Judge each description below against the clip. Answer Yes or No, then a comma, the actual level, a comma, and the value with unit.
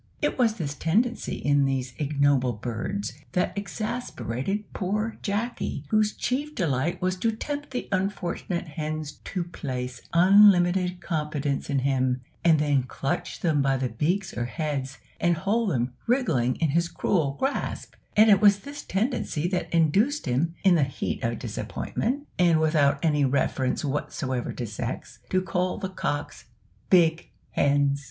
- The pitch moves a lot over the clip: Yes, wide, 6.4 semitones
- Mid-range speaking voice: Yes, medium, 165 Hz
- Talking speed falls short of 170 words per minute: Yes, average, 150 wpm